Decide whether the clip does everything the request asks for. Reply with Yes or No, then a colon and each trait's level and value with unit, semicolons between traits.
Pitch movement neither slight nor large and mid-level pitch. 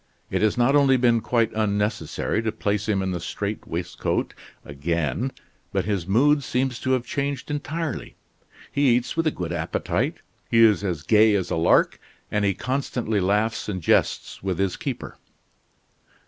No: average, 4.8 semitones; low, 110 Hz